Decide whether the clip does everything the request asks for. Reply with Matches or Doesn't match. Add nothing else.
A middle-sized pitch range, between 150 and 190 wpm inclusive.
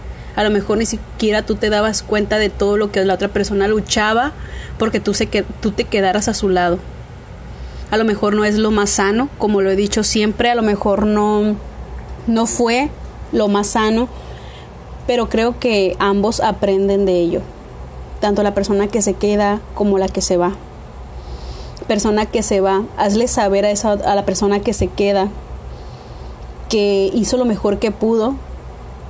Doesn't match